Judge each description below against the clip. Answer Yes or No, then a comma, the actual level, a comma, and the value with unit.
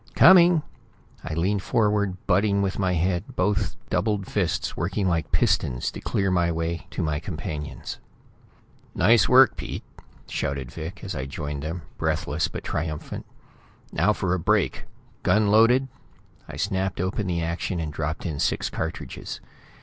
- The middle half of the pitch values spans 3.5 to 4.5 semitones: Yes, average, 4.1 semitones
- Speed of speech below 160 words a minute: Yes, average, 150 wpm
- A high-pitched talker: No, very low, 90 Hz